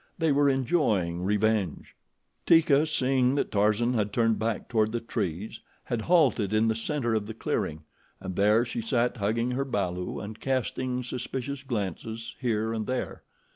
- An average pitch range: Yes, average, 3.6 semitones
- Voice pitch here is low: Yes, low, 115 Hz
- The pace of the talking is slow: No, average, 160 wpm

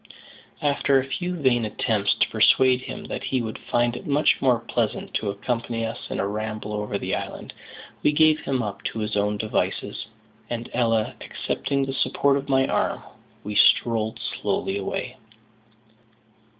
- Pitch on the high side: No, low, 120 Hz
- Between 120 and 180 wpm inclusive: Yes, average, 165 wpm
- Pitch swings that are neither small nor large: Yes, average, 3.9 semitones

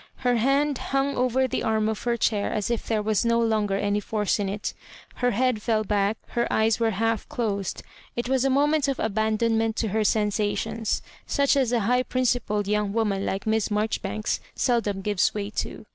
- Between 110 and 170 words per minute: No, average, 200 wpm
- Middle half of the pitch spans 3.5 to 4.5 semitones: No, average, 2.8 semitones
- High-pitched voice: Yes, high, 220 Hz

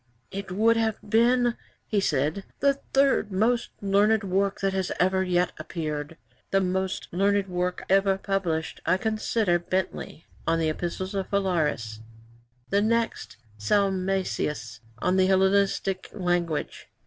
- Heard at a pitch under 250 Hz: Yes, high, 190 Hz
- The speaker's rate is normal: No, slow, 130 wpm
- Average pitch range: No, narrow, 2.3 semitones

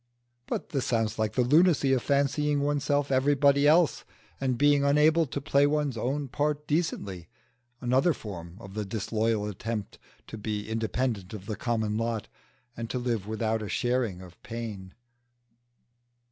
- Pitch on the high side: No, low, 120 Hz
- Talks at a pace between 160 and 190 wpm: No, average, 150 wpm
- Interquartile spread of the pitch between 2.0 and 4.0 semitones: No, average, 4.8 semitones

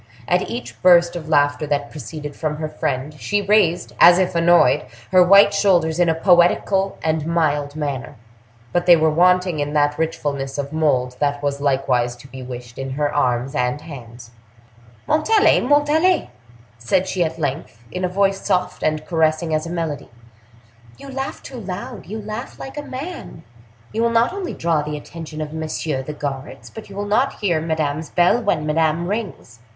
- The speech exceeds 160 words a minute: Yes, average, 175 wpm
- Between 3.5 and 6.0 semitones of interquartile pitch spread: Yes, average, 4.6 semitones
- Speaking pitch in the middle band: Yes, medium, 160 Hz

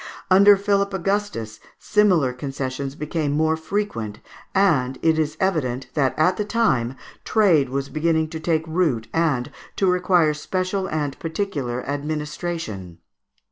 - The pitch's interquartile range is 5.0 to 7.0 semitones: Yes, wide, 5.5 semitones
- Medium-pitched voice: Yes, medium, 155 Hz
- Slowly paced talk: Yes, slow, 130 wpm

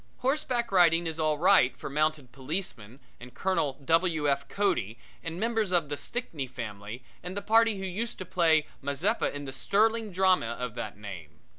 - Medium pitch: Yes, medium, 160 Hz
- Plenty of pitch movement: Yes, wide, 6.8 semitones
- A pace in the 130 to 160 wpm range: No, average, 175 wpm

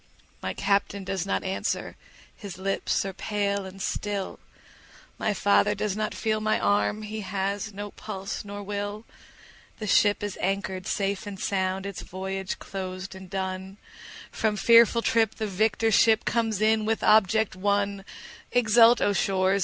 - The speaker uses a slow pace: No, average, 155 wpm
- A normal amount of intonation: No, narrow, 2.0 semitones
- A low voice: No, high, 200 Hz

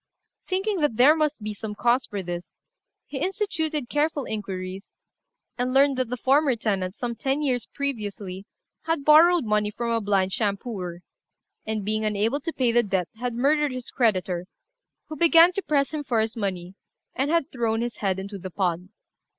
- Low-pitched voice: No, high, 235 Hz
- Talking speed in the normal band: Yes, average, 175 wpm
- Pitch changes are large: Yes, wide, 6.2 semitones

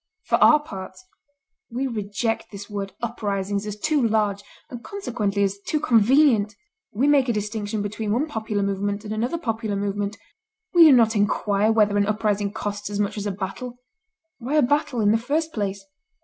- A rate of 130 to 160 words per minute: No, average, 175 wpm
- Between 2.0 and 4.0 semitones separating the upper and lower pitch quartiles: Yes, average, 3.2 semitones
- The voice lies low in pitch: No, high, 215 Hz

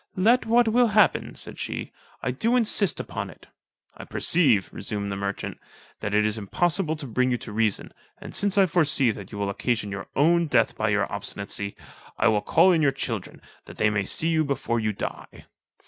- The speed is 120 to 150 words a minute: No, average, 200 wpm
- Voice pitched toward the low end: Yes, low, 125 Hz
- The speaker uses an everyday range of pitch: No, wide, 8.7 semitones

